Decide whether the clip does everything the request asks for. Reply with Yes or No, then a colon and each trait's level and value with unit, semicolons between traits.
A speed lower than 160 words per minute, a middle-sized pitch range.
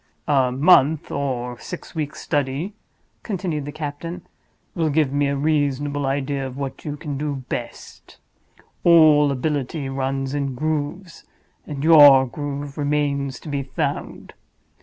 No: slow, 135 wpm; narrow, 1.9 semitones